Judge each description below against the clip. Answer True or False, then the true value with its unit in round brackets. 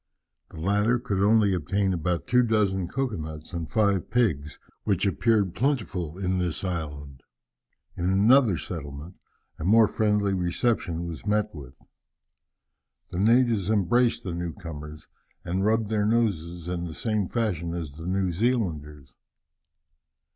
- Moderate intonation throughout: True (4.4 semitones)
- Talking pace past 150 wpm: False (140 wpm)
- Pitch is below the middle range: True (95 Hz)